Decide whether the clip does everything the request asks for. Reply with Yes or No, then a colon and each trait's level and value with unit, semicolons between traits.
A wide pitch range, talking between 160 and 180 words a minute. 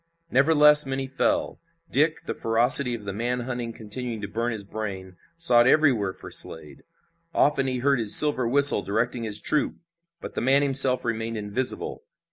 No: average, 3.8 semitones; average, 165 wpm